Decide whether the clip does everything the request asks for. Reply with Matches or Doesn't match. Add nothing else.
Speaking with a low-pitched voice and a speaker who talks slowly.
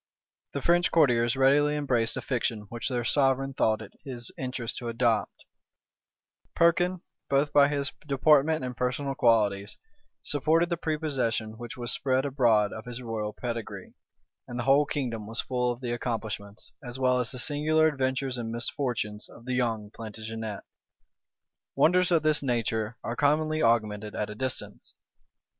Doesn't match